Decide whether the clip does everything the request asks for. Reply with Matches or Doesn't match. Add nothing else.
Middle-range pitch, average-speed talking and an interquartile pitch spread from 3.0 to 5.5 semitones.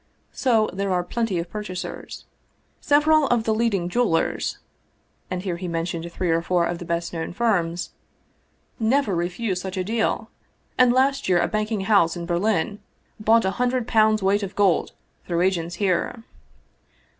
Doesn't match